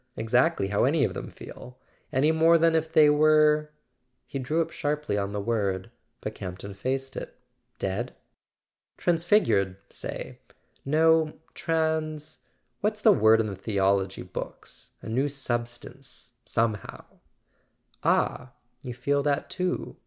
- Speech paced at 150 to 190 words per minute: No, slow, 135 wpm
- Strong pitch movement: Yes, wide, 6.1 semitones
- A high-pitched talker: No, low, 135 Hz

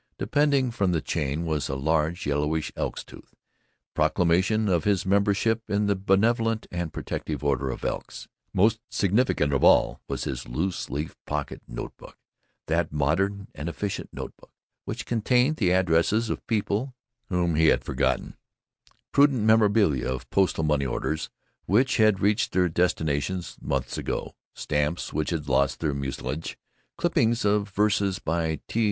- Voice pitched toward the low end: Yes, very low, 90 Hz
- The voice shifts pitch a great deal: Yes, wide, 5.8 semitones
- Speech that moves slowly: No, average, 150 wpm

